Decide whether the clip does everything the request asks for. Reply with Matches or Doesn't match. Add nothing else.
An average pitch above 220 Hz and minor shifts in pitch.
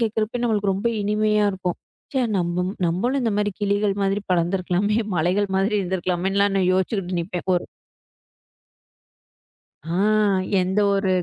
Doesn't match